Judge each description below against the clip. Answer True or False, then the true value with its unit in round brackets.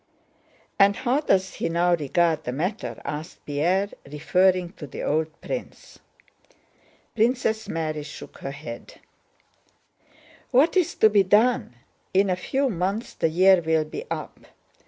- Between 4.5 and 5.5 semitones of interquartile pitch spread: True (5.1 semitones)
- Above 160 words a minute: False (135 wpm)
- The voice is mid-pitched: True (180 Hz)